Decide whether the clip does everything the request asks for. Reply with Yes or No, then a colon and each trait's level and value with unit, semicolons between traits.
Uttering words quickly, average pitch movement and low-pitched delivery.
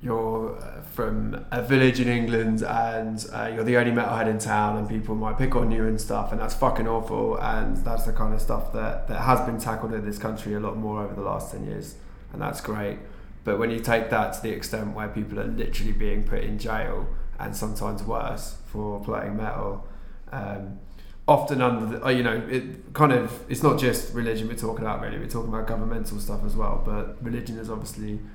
No: fast, 215 wpm; narrow, 1.8 semitones; low, 110 Hz